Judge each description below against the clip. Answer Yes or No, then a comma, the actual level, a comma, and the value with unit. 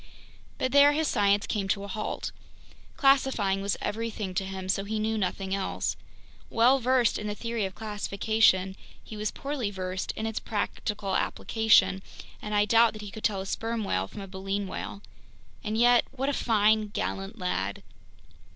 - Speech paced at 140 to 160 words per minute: No, average, 175 wpm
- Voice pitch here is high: Yes, high, 210 Hz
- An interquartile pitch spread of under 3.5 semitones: Yes, average, 2.7 semitones